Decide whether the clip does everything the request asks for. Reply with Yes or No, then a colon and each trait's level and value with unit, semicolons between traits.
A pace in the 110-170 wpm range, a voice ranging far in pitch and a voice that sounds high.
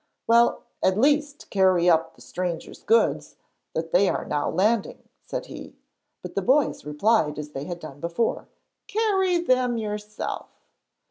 Yes: average, 140 wpm; wide, 7.4 semitones; high, 205 Hz